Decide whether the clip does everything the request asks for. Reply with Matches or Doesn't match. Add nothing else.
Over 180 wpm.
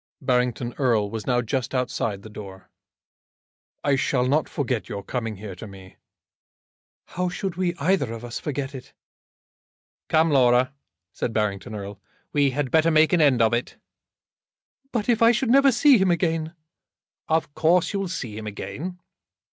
Doesn't match